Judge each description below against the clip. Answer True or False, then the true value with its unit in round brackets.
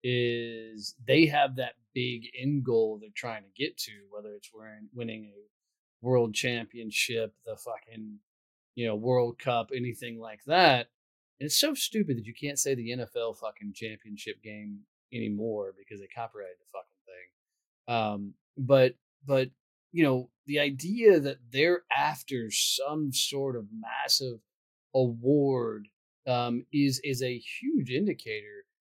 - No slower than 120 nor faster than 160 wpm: True (150 wpm)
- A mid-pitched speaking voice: False (120 Hz)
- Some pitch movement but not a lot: True (4.1 semitones)